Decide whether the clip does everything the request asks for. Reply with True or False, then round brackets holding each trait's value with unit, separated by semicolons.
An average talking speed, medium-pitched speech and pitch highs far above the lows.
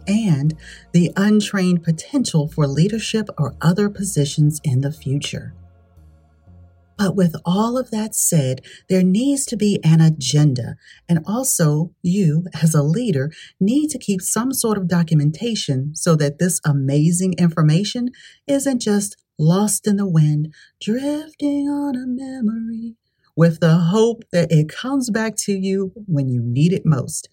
True (145 wpm; 175 Hz; 6.2 semitones)